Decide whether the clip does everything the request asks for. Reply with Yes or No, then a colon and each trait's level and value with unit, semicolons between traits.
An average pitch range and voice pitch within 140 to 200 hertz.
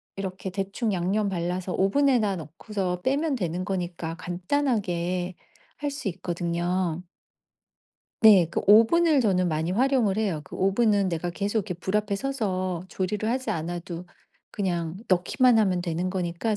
Yes: average, 3.6 semitones; high, 190 Hz